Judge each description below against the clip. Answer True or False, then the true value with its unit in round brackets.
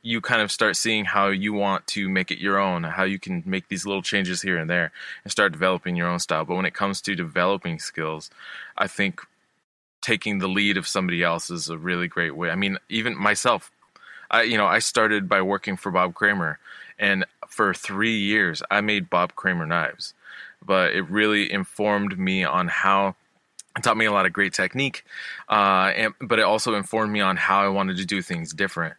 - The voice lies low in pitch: True (95 Hz)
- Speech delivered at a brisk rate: True (210 wpm)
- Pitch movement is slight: True (1.9 semitones)